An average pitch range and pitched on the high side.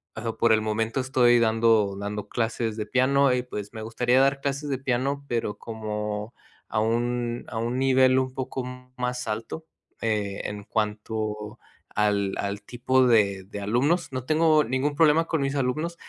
No: average, 3.6 semitones; low, 120 Hz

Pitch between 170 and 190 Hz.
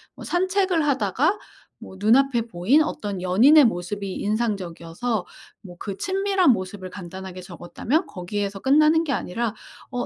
No: high, 215 Hz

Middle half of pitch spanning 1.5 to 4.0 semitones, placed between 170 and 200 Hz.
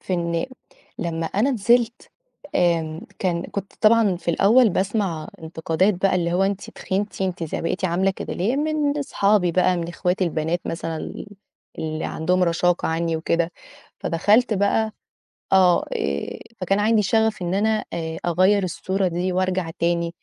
Yes: average, 3.2 semitones; medium, 185 Hz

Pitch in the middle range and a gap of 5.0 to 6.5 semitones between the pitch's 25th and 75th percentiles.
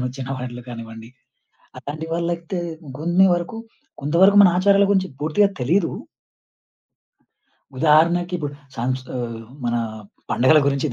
Yes: medium, 155 Hz; wide, 5.6 semitones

